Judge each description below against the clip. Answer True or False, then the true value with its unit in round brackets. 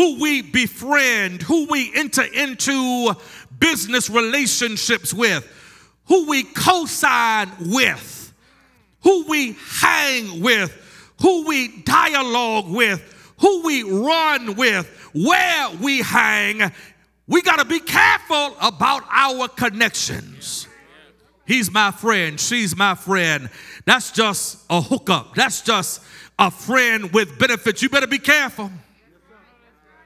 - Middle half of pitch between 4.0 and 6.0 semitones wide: True (5.2 semitones)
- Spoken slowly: True (115 wpm)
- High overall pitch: True (250 Hz)